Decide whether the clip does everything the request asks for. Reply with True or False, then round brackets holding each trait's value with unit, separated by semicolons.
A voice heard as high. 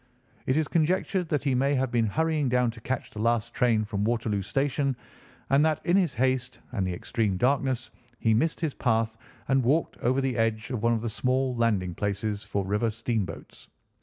False (120 Hz)